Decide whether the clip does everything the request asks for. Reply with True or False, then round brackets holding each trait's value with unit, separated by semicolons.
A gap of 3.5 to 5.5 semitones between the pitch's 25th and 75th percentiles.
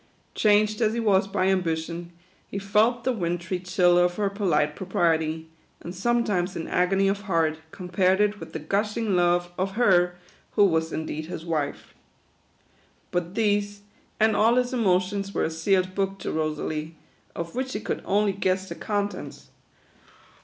False (3.1 semitones)